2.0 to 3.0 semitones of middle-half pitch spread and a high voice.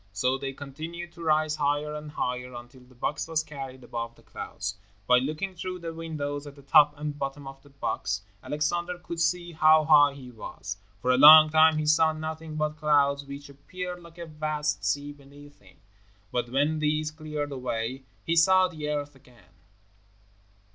No: narrow, 2.5 semitones; medium, 150 Hz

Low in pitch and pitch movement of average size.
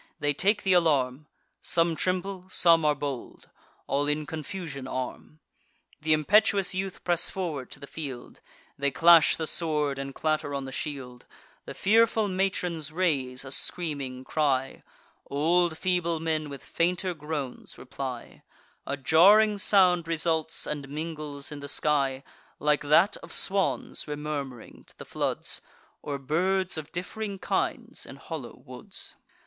No: medium, 155 Hz; average, 4.0 semitones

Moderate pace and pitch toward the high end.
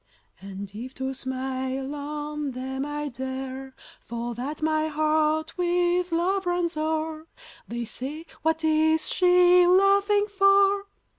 No: slow, 125 wpm; very high, 310 Hz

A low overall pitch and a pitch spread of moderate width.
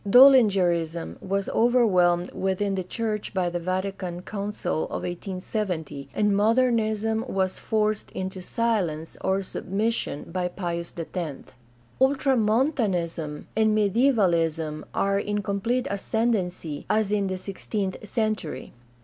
No: high, 195 Hz; average, 3.6 semitones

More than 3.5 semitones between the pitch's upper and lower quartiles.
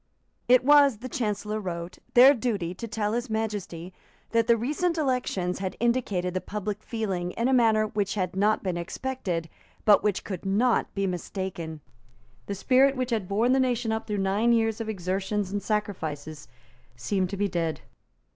Yes: average, 4.1 semitones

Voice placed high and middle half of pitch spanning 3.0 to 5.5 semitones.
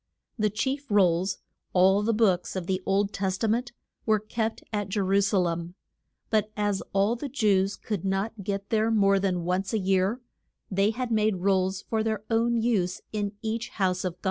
No: high, 200 Hz; narrow, 2.6 semitones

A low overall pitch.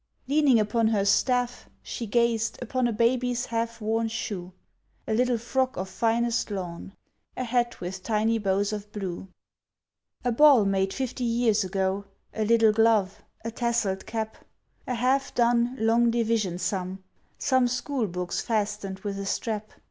No: high, 225 Hz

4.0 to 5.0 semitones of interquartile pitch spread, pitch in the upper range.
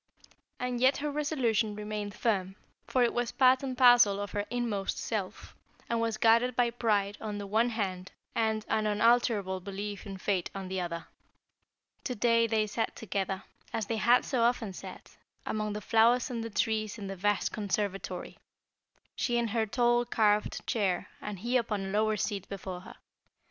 No: average, 2.9 semitones; high, 215 Hz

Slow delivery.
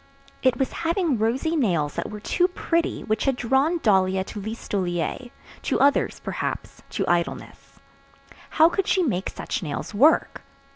No: average, 150 wpm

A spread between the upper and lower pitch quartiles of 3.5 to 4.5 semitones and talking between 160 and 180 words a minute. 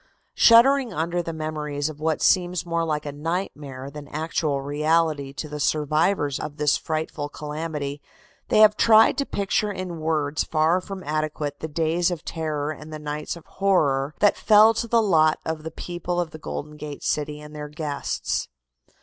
No: average, 2.8 semitones; average, 175 wpm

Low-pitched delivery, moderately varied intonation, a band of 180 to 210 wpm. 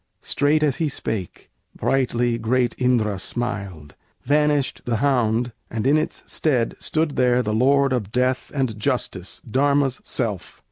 No: low, 125 Hz; average, 3.9 semitones; average, 140 wpm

